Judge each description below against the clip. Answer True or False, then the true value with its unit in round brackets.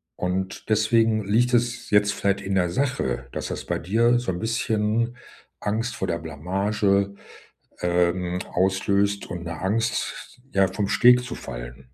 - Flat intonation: False (3.9 semitones)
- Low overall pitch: True (100 Hz)